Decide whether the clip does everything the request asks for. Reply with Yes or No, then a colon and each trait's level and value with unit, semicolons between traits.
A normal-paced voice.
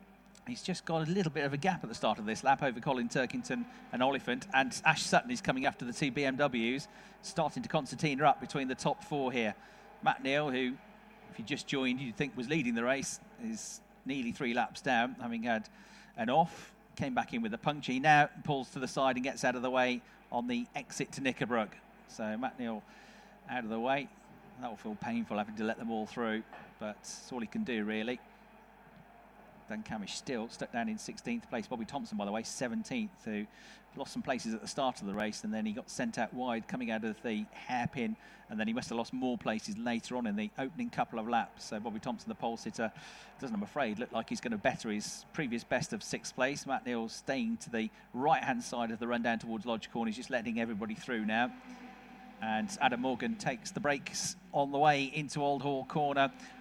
No: fast, 225 wpm